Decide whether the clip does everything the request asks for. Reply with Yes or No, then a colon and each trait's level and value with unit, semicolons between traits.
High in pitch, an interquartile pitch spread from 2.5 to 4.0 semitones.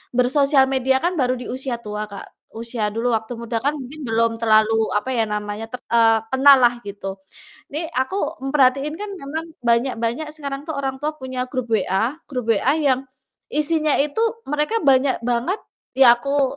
Yes: very high, 255 Hz; average, 3.5 semitones